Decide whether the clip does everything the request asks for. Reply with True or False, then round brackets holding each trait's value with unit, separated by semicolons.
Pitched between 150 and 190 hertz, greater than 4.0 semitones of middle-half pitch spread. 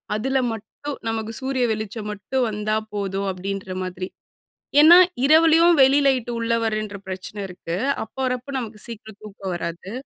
False (215 Hz; 4.6 semitones)